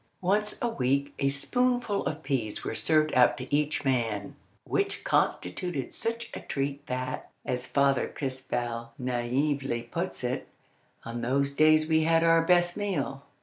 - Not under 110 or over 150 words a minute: Yes, average, 145 wpm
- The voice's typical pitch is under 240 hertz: Yes, medium, 140 Hz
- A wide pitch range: No, average, 4.4 semitones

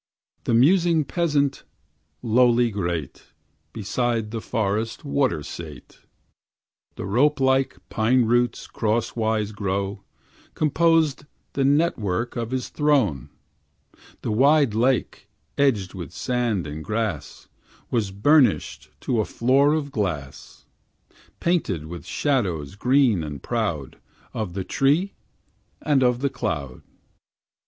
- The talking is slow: Yes, slow, 110 wpm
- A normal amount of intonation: No, wide, 5.9 semitones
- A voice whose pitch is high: No, low, 115 Hz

